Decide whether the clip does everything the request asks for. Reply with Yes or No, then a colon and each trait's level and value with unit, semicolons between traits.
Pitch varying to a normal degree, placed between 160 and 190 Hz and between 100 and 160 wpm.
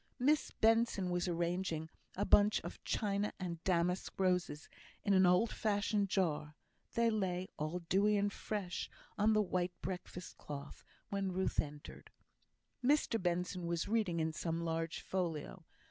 Yes: average, 3.2 semitones; medium, 185 Hz; average, 145 wpm